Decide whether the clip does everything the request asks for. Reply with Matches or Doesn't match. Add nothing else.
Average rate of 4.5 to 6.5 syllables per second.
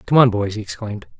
Doesn't match